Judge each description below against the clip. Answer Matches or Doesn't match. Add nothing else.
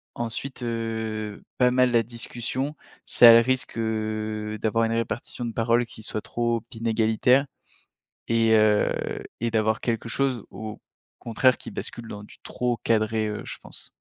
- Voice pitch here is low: Matches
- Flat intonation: Matches